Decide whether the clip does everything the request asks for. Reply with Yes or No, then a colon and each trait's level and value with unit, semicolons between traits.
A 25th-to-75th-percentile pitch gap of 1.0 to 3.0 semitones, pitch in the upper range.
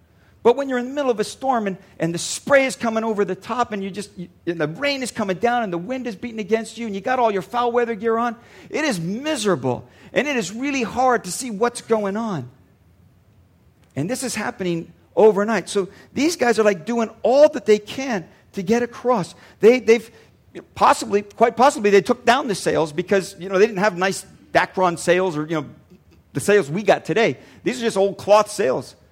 No: average, 4.7 semitones; high, 215 Hz